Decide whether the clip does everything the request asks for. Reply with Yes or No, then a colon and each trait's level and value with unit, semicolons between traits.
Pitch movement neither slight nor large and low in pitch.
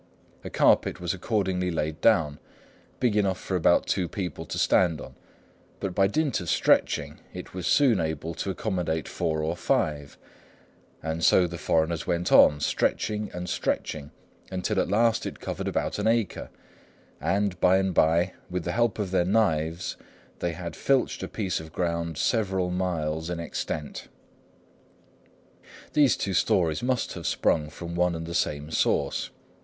Yes: average, 3.1 semitones; very low, 90 Hz